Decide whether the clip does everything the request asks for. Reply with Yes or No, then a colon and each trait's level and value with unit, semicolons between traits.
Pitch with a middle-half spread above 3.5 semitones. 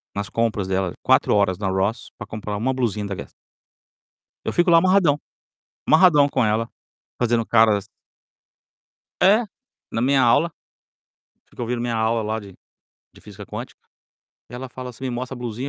Yes: average, 3.9 semitones